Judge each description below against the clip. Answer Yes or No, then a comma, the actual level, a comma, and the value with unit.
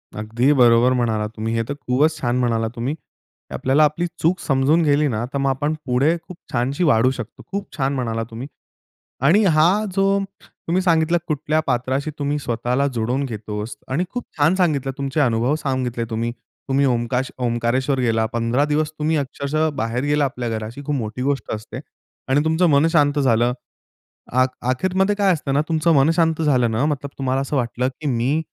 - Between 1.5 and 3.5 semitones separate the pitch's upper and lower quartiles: No, average, 4.1 semitones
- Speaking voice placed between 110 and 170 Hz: Yes, low, 135 Hz